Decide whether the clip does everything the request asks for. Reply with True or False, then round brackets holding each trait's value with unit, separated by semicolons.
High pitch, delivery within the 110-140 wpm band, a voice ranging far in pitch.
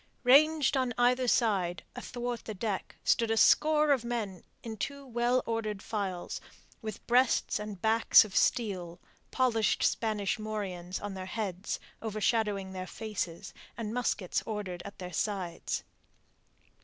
False (215 Hz; 135 wpm; 3.9 semitones)